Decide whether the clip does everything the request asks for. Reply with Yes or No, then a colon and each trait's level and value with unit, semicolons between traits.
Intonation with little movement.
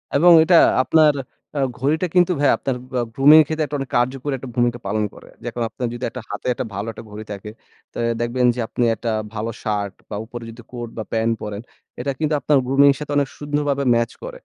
No: average, 4.2 semitones